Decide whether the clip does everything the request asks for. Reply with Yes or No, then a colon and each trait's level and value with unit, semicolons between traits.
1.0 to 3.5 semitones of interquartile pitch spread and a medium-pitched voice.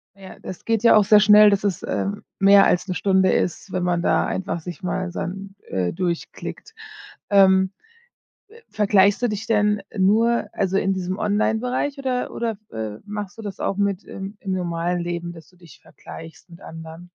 No: average, 2.8 semitones; high, 195 Hz